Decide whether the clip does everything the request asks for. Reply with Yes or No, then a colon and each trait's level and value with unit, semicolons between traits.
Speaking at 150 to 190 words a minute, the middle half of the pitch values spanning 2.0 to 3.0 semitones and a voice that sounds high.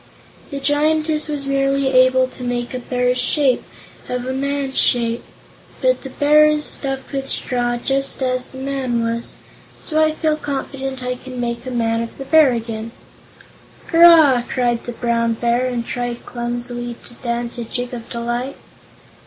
Yes: average, 165 wpm; narrow, 2.4 semitones; very high, 255 Hz